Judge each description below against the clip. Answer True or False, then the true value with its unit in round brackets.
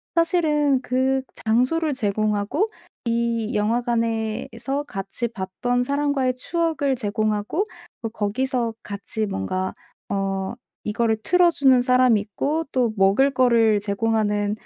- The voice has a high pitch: True (235 Hz)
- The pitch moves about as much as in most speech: True (4.2 semitones)